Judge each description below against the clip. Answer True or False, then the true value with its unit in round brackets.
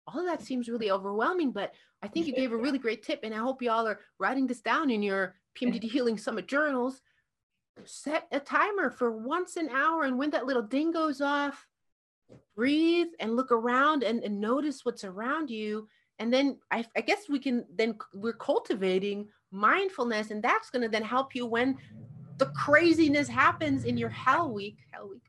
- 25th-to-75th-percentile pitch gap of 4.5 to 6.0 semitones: True (5.2 semitones)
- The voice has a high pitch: True (250 Hz)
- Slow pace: False (195 wpm)